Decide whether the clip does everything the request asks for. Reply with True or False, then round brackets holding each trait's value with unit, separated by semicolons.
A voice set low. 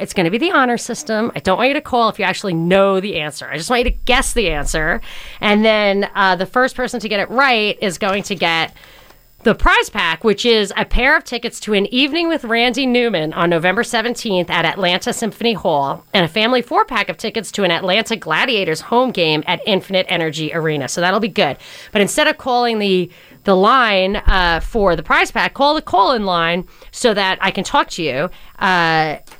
False (200 Hz)